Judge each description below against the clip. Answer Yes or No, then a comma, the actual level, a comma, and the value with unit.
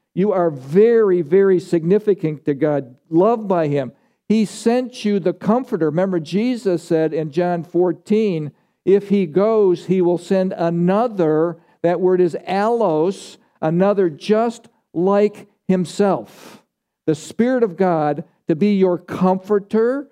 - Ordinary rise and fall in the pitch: Yes, average, 3.6 semitones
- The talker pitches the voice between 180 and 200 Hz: Yes, medium, 185 Hz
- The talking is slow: Yes, slow, 130 wpm